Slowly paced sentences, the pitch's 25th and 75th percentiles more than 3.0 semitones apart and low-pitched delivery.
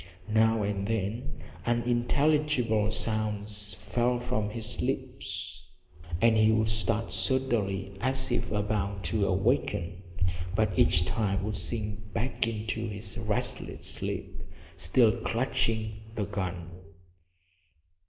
No: slow, 110 wpm; narrow, 2.5 semitones; low, 110 Hz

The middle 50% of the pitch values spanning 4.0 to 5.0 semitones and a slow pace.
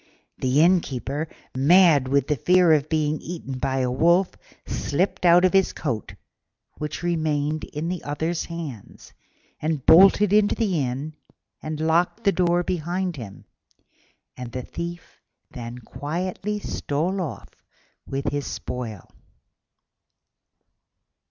Yes: average, 4.3 semitones; slow, 125 wpm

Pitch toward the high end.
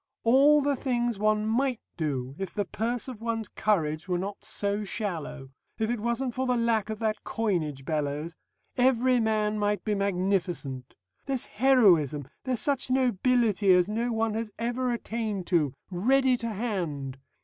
Yes: high, 215 Hz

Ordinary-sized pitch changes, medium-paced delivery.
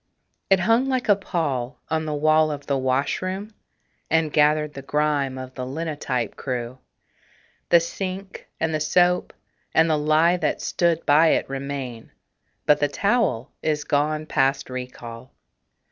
Yes: average, 3.7 semitones; average, 145 wpm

